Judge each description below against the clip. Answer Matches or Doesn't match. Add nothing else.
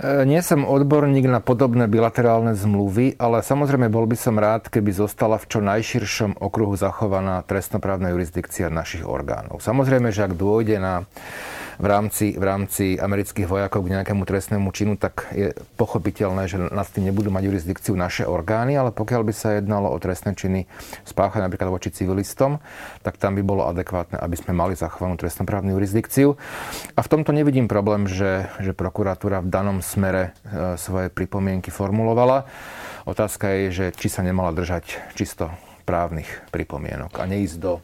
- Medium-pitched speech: Doesn't match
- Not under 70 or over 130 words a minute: Doesn't match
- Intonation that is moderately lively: Matches